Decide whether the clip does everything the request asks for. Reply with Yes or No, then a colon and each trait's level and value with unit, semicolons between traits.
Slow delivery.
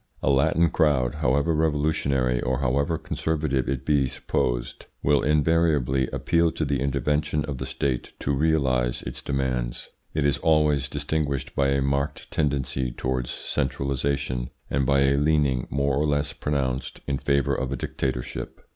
No: average, 150 wpm